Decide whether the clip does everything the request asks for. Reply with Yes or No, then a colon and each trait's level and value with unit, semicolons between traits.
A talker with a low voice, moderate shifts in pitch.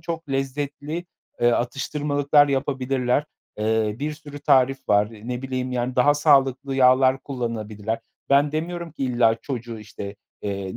Yes: low, 130 Hz; average, 3.5 semitones